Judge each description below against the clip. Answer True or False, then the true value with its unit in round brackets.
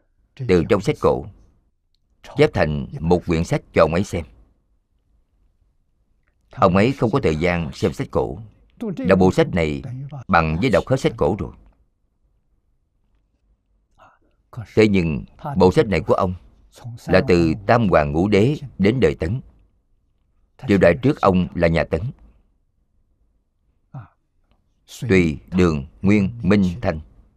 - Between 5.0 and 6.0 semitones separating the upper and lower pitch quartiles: False (4.1 semitones)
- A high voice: False (90 Hz)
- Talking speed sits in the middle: False (135 wpm)